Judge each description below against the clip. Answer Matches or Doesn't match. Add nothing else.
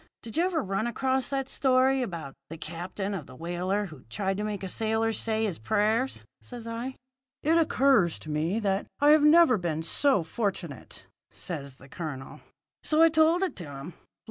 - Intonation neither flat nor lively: Doesn't match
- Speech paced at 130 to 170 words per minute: Doesn't match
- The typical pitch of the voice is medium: Doesn't match